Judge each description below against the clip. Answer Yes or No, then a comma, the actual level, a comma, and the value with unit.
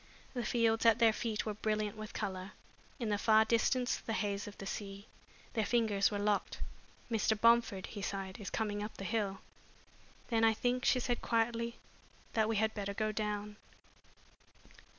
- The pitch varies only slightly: Yes, narrow, 1.9 semitones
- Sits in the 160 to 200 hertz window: No, high, 215 Hz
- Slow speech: No, average, 170 wpm